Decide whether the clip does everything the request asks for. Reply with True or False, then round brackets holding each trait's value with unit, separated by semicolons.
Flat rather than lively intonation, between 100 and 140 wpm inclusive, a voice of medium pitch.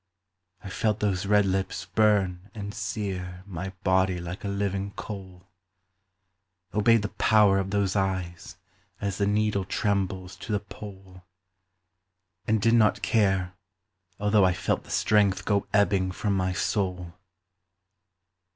False (1.9 semitones; 135 wpm; 100 Hz)